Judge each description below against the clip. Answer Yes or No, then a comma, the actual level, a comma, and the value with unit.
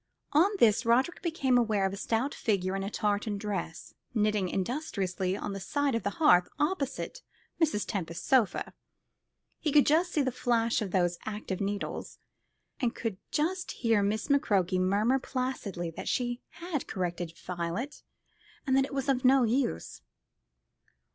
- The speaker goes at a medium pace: Yes, average, 155 wpm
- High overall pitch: Yes, high, 225 Hz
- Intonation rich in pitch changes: Yes, wide, 5.7 semitones